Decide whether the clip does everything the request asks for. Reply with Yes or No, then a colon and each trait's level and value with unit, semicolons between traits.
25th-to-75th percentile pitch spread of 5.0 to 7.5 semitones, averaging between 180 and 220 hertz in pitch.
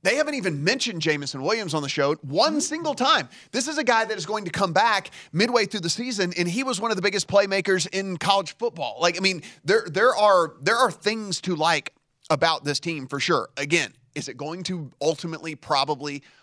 Yes: wide, 5.6 semitones; medium, 185 Hz